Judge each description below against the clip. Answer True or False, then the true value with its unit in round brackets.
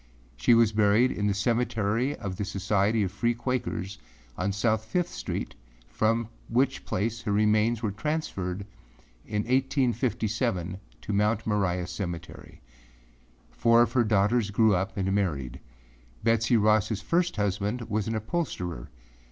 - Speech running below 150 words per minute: True (135 wpm)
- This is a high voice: False (105 Hz)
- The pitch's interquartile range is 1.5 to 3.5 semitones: True (2.8 semitones)